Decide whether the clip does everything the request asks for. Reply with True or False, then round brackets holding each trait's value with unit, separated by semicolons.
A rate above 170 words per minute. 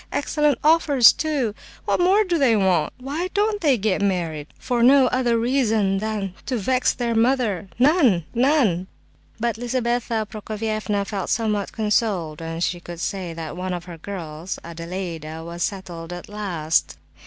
False (145 wpm)